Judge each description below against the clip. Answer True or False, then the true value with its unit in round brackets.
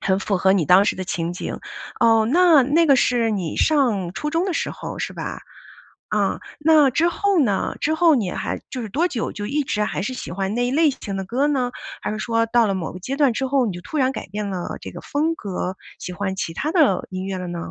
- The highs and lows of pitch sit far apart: True (7.1 semitones)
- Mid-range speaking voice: False (230 Hz)